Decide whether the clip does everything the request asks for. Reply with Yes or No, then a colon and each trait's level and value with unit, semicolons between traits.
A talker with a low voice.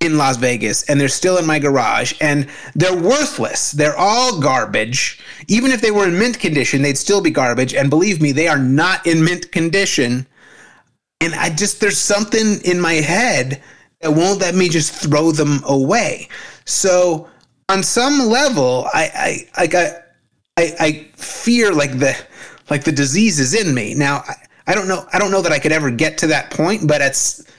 No: medium, 165 Hz